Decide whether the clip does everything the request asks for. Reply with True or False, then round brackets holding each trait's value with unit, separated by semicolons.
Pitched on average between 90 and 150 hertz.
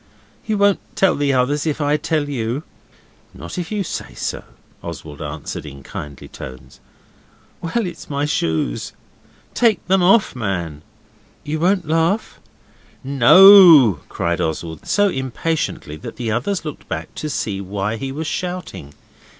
True (140 Hz)